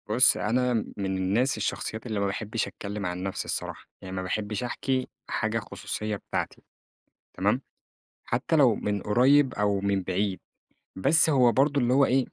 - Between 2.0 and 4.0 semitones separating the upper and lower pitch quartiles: No, average, 4.4 semitones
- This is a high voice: No, low, 110 Hz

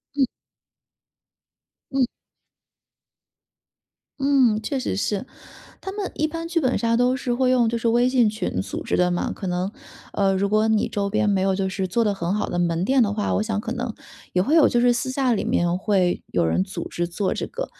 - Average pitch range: Yes, average, 4.8 semitones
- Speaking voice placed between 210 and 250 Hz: Yes, high, 215 Hz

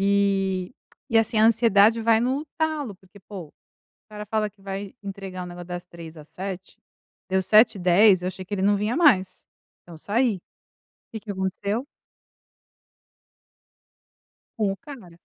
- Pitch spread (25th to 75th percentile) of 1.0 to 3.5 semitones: Yes, average, 3.0 semitones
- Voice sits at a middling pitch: No, high, 200 Hz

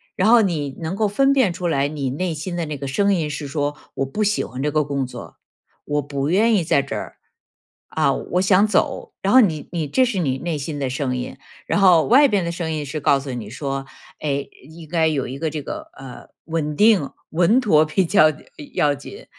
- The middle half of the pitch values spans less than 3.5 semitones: No, average, 5.0 semitones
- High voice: No, medium, 155 Hz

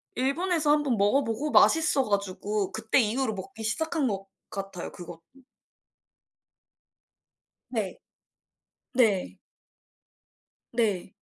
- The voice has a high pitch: Yes, high, 220 Hz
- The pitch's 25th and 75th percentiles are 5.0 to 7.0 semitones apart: Yes, wide, 5.5 semitones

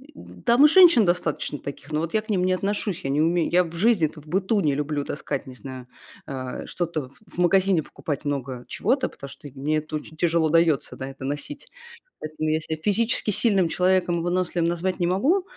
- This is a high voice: No, medium, 170 Hz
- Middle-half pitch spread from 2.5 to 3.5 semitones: No, average, 4.4 semitones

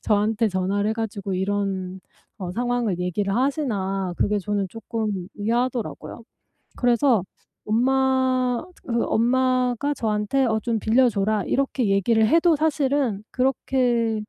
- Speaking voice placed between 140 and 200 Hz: No, high, 225 Hz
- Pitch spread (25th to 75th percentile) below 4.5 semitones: Yes, average, 3.9 semitones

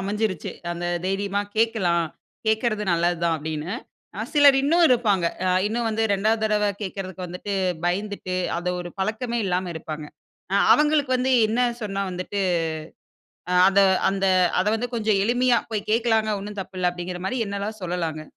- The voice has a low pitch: No, high, 200 Hz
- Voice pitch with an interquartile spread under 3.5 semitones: No, average, 3.8 semitones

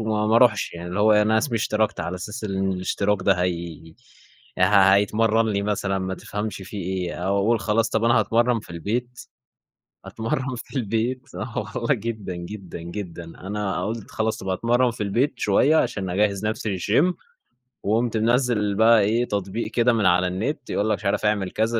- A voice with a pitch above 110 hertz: No, low, 105 Hz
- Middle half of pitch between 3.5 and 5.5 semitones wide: No, average, 3.1 semitones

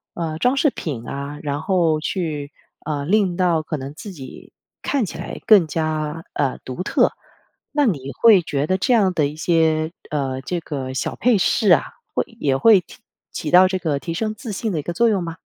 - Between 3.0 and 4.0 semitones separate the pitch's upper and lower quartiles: No, average, 4.7 semitones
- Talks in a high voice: No, medium, 165 Hz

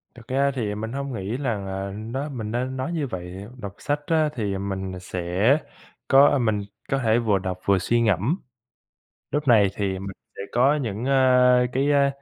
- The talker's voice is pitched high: No, low, 115 Hz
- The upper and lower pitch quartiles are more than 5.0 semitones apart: Yes, wide, 5.4 semitones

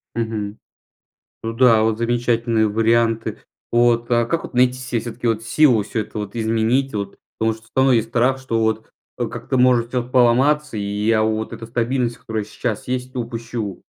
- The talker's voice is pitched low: Yes, low, 115 Hz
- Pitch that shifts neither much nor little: No, narrow, 1.8 semitones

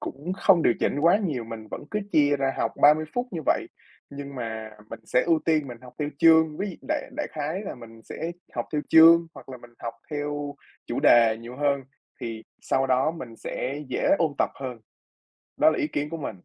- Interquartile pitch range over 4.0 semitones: Yes, average, 4.6 semitones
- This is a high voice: No, medium, 145 Hz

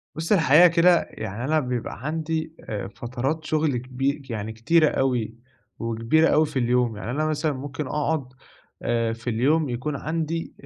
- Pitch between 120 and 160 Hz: Yes, medium, 140 Hz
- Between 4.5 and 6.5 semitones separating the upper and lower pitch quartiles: Yes, average, 4.8 semitones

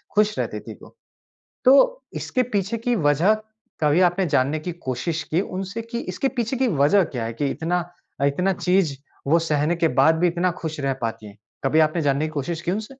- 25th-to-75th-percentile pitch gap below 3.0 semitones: No, average, 5.2 semitones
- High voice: No, medium, 165 Hz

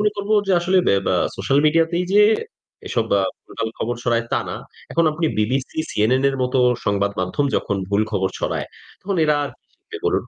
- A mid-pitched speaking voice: No, low, 130 Hz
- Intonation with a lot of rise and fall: Yes, wide, 7.7 semitones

